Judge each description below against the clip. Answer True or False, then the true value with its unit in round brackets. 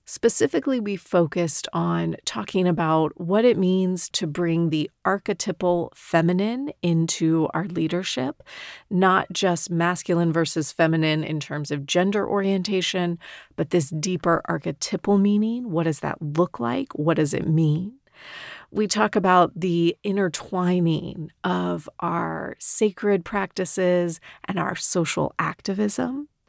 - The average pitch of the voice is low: False (175 Hz)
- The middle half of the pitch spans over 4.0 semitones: False (3.2 semitones)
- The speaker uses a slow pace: True (120 wpm)